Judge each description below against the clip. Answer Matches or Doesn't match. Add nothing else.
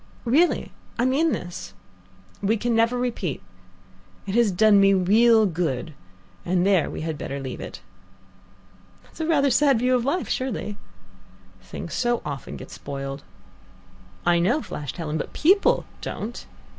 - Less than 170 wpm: Matches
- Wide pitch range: Matches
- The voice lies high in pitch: Matches